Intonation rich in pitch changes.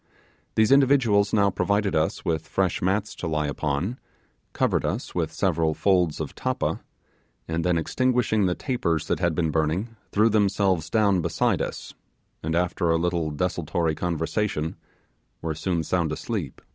No: average, 4.1 semitones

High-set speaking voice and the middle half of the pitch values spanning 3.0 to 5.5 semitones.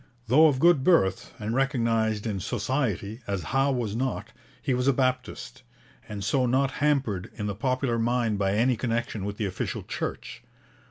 No: low, 120 Hz; average, 4.0 semitones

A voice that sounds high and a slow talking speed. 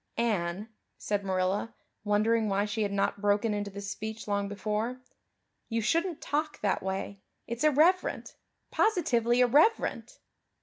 Yes: high, 215 Hz; slow, 130 wpm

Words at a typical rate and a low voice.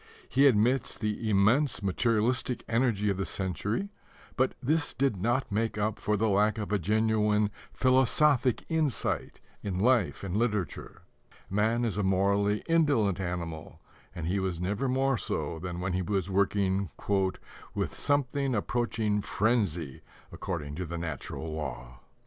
Yes: average, 145 wpm; low, 105 Hz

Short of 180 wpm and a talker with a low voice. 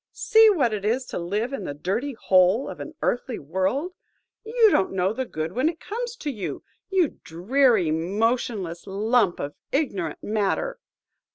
No: average, 165 wpm; high, 225 Hz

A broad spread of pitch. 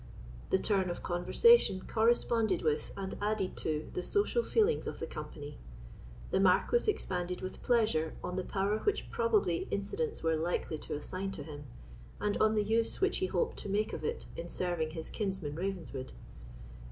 No: average, 4.8 semitones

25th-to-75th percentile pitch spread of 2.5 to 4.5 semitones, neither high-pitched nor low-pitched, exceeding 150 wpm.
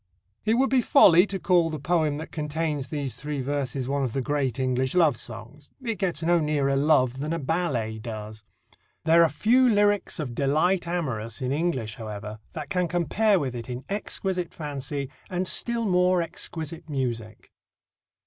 No: average, 5.2 semitones; medium, 150 Hz; average, 170 wpm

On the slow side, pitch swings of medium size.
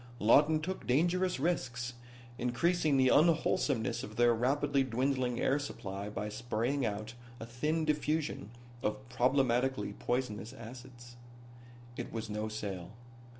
Yes: slow, 120 wpm; average, 4.3 semitones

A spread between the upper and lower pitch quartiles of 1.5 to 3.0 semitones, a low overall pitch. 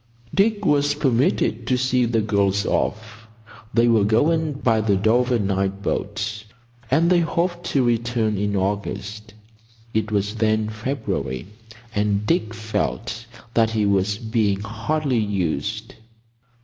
No: average, 3.4 semitones; low, 110 Hz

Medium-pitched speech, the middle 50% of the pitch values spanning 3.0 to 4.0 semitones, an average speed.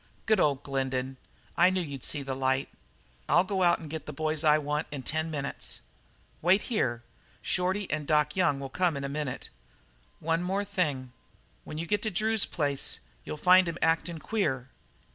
No: medium, 155 Hz; average, 4.5 semitones; average, 180 wpm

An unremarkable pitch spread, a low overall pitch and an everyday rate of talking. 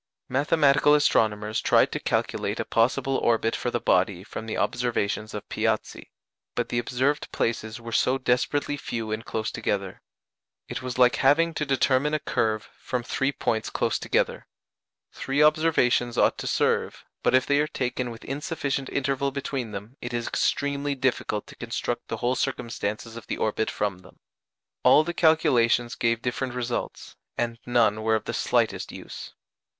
Yes: average, 3.5 semitones; low, 120 Hz; average, 165 wpm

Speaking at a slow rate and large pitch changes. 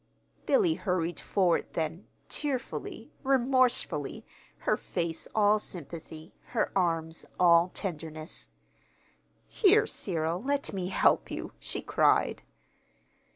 Yes: slow, 100 wpm; wide, 7.2 semitones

